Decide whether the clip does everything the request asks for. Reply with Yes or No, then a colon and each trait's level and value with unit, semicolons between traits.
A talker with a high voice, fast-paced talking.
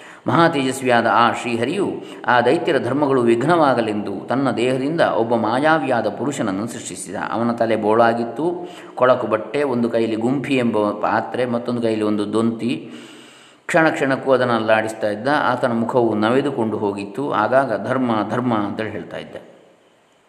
No: low, 115 Hz; fast, 120 wpm